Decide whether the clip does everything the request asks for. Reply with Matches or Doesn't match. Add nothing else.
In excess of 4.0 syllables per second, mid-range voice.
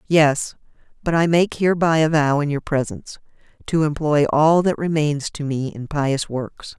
Matches